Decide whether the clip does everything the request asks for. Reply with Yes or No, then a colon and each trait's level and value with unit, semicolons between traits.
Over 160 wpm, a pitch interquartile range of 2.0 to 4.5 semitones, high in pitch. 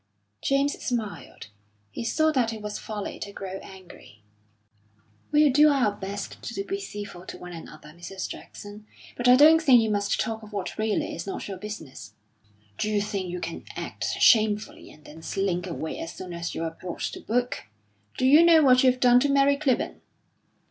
No: average, 185 wpm; average, 5.3 semitones; high, 210 Hz